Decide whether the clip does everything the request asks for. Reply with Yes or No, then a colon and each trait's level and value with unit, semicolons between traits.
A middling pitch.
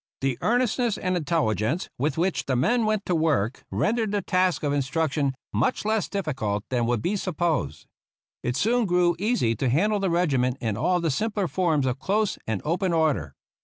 Yes: medium, 170 Hz